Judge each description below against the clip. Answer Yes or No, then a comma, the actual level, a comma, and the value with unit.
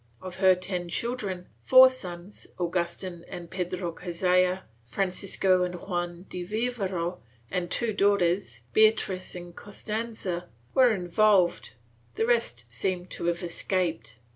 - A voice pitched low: No, medium, 180 Hz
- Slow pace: Yes, slow, 120 wpm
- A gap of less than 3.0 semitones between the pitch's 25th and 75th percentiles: Yes, narrow, 2.5 semitones